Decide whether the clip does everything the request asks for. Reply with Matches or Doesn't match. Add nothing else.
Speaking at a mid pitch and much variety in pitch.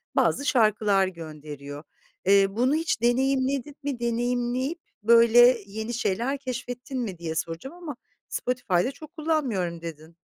Doesn't match